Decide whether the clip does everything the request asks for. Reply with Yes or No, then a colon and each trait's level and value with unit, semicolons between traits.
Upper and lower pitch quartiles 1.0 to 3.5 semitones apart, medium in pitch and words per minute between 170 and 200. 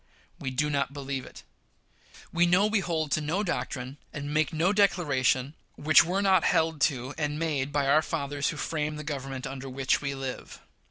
Yes: average, 3.2 semitones; medium, 150 Hz; average, 185 wpm